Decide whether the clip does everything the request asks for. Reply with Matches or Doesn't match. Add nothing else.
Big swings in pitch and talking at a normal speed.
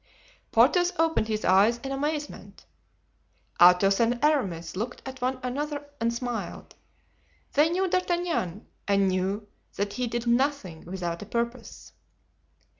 Doesn't match